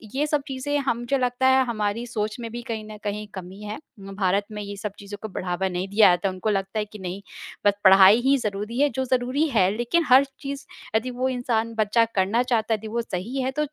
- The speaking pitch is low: No, high, 220 Hz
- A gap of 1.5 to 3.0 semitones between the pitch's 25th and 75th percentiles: No, average, 4.0 semitones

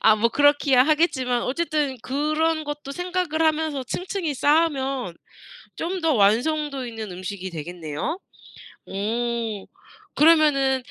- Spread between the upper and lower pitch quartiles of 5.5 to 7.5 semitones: No, average, 5.1 semitones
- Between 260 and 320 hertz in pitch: Yes, very high, 275 Hz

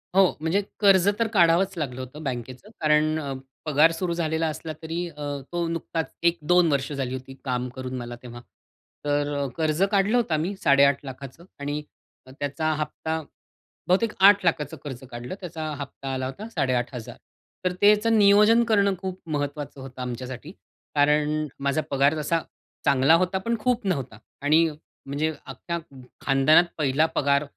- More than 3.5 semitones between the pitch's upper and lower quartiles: Yes, average, 4.3 semitones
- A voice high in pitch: No, medium, 155 Hz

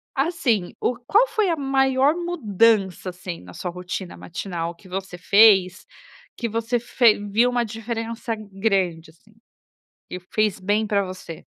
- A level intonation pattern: No, average, 4.6 semitones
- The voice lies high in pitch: Yes, high, 210 Hz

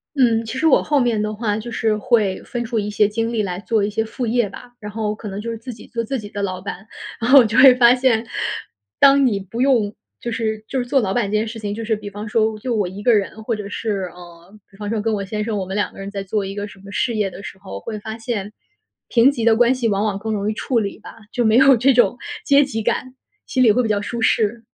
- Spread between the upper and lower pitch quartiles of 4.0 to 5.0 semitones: No, narrow, 2.6 semitones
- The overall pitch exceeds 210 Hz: Yes, high, 220 Hz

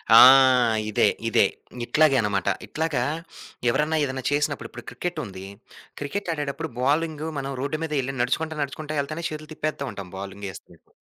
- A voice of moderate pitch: Yes, medium, 145 Hz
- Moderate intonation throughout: Yes, average, 3.7 semitones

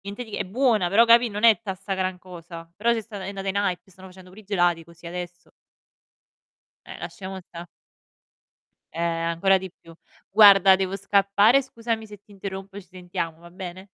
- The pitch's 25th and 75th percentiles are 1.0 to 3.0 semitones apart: Yes, narrow, 2.5 semitones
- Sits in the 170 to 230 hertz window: Yes, high, 190 Hz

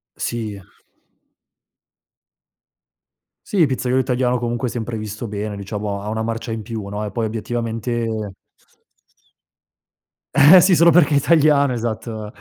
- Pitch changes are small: No, average, 3.2 semitones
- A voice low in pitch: Yes, low, 115 Hz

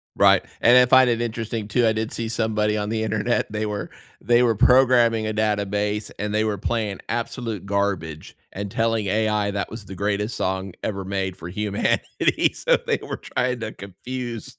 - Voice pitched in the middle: No, low, 110 Hz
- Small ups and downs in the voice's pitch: Yes, narrow, 2.3 semitones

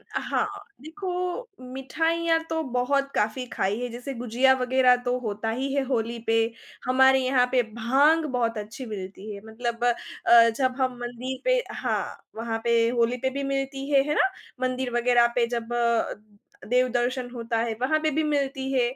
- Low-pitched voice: No, very high, 250 Hz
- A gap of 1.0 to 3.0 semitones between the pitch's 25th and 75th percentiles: Yes, narrow, 2.4 semitones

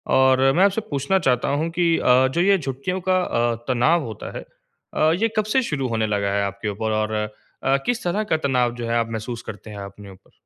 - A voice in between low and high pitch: No, low, 125 Hz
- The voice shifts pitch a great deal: Yes, wide, 7.4 semitones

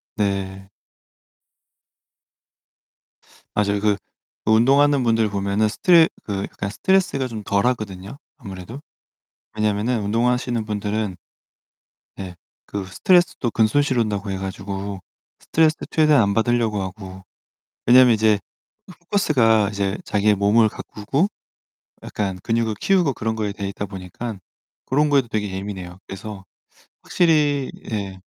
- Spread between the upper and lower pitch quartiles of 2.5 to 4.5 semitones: Yes, average, 3.8 semitones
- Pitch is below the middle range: Yes, low, 110 Hz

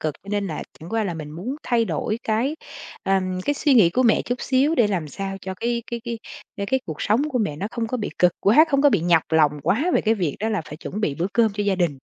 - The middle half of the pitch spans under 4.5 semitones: No, average, 5.3 semitones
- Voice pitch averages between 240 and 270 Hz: No, high, 205 Hz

